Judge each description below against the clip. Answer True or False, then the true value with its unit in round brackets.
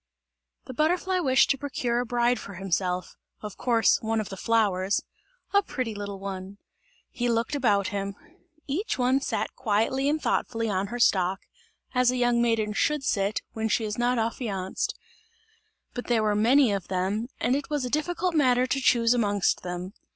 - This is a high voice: True (230 Hz)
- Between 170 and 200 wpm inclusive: True (175 wpm)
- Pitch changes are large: False (4.2 semitones)